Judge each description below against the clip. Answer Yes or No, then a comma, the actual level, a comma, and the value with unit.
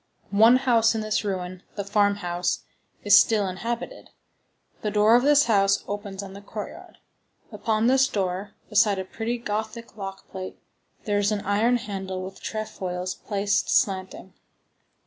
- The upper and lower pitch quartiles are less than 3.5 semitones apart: Yes, narrow, 2.4 semitones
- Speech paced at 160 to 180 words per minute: No, average, 145 wpm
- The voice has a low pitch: No, high, 205 Hz